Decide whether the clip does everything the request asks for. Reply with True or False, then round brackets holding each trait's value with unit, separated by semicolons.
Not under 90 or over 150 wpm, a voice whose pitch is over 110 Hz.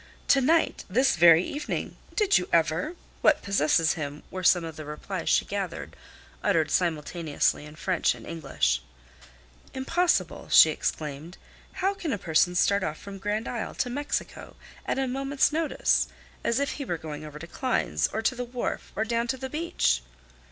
False (175 wpm; 190 Hz)